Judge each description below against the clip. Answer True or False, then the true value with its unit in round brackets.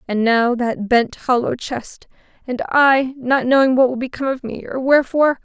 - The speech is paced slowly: False (190 wpm)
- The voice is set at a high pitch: True (255 Hz)